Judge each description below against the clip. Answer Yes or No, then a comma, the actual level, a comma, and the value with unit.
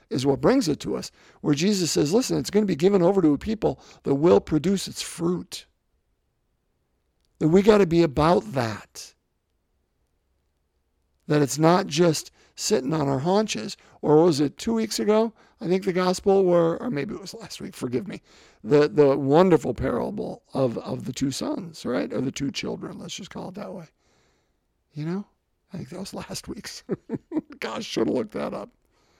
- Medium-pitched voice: Yes, medium, 170 Hz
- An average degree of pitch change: No, wide, 5.9 semitones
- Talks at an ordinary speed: Yes, average, 190 wpm